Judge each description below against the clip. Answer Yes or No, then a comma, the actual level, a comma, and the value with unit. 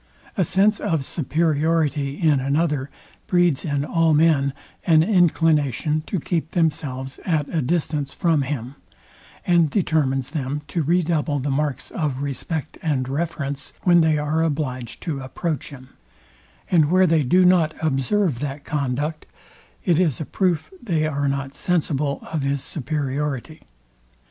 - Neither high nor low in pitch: Yes, medium, 150 Hz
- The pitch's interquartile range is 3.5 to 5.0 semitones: No, average, 3.0 semitones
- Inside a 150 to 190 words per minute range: No, average, 140 wpm